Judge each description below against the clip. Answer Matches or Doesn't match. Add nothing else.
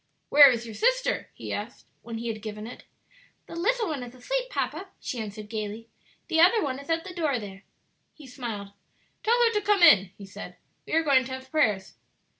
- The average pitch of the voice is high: Matches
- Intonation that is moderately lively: Doesn't match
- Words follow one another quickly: Matches